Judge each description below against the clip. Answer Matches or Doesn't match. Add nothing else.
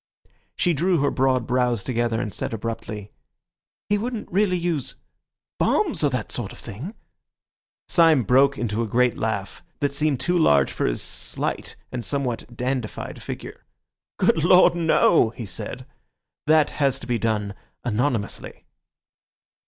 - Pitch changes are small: Doesn't match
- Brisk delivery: Doesn't match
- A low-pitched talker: Matches